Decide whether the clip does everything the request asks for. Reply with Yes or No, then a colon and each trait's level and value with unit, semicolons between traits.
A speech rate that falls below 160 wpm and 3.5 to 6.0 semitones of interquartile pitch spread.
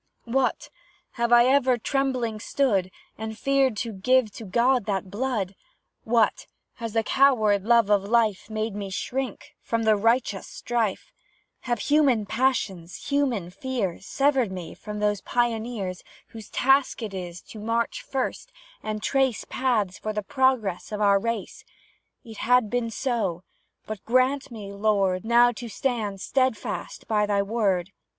Yes: average, 145 wpm; average, 3.8 semitones